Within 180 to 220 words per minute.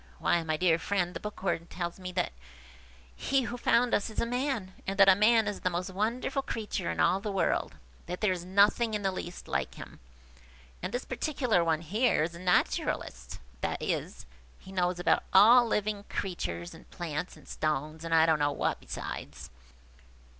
Yes: average, 190 wpm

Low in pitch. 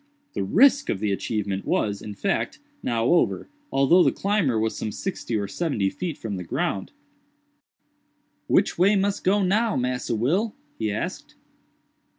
Yes: low, 125 Hz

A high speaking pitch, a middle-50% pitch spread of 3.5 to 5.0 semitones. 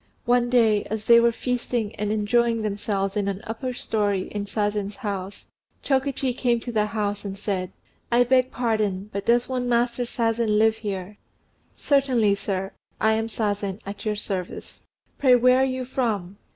No: high, 220 Hz; average, 3.1 semitones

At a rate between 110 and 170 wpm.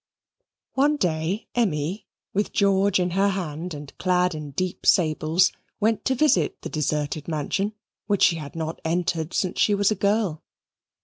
Yes: average, 160 wpm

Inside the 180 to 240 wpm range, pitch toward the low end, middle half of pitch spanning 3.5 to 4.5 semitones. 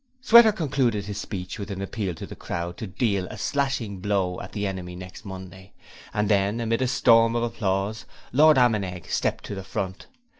Yes: average, 190 wpm; low, 100 Hz; average, 3.8 semitones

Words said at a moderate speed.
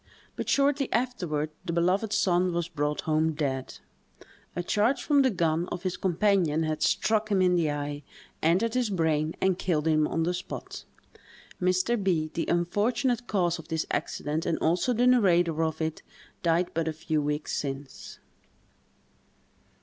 Yes: average, 160 wpm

